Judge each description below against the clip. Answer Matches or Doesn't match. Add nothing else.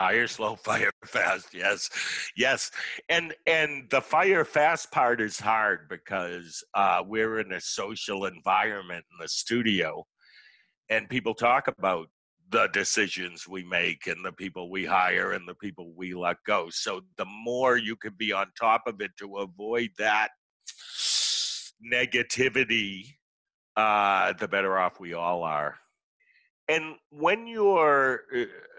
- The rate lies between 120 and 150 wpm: Matches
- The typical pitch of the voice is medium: Doesn't match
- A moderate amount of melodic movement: Doesn't match